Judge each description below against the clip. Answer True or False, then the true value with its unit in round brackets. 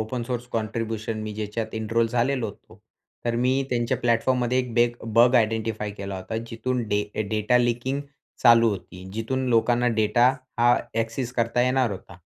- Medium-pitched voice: False (115 Hz)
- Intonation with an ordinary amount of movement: False (1.9 semitones)